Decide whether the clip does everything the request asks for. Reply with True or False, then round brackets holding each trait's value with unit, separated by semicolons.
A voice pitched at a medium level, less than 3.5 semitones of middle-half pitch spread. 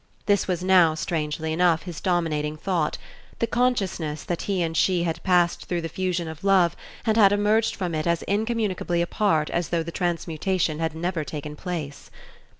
True (175 Hz; 2.9 semitones)